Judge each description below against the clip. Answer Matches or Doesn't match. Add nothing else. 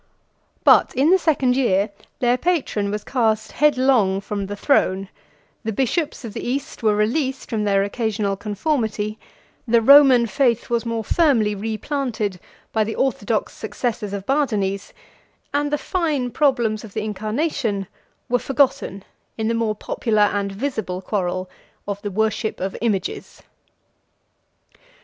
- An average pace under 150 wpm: Matches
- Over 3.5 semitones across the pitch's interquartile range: Matches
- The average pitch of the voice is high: Matches